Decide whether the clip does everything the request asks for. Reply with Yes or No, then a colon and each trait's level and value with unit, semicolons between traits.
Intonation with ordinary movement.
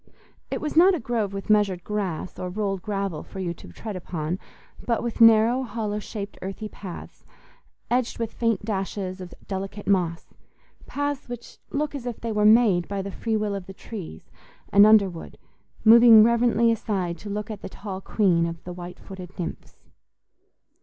Yes: average, 3.4 semitones